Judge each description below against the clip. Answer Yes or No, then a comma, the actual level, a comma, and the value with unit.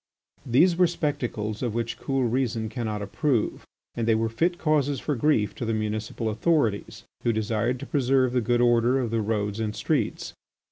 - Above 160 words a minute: Yes, average, 180 wpm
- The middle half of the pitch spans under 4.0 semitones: Yes, average, 3.5 semitones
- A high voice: No, low, 120 Hz